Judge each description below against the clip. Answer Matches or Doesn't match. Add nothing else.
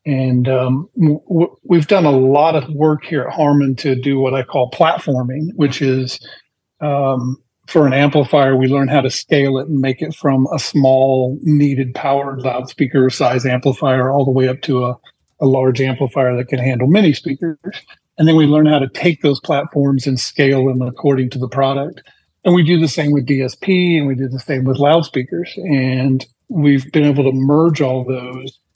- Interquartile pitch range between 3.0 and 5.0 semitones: Doesn't match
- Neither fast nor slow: Matches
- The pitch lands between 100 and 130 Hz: Doesn't match